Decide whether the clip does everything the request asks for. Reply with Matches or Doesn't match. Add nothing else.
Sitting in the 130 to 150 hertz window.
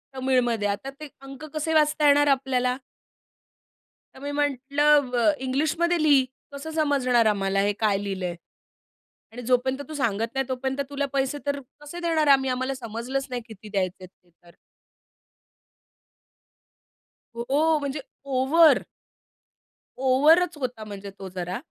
Doesn't match